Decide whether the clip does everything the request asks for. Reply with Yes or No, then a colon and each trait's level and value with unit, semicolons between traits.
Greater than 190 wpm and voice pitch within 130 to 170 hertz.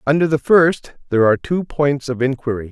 Yes: average, 200 wpm; medium, 140 Hz